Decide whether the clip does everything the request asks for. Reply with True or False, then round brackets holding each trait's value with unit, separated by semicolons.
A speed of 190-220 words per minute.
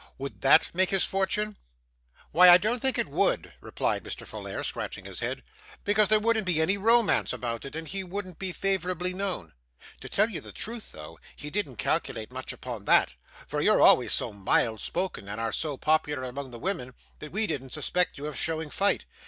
True (200 wpm)